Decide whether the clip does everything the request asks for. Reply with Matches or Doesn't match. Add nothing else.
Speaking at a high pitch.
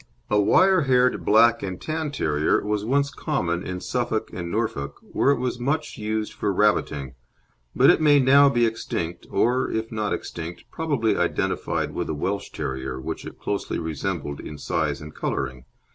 Doesn't match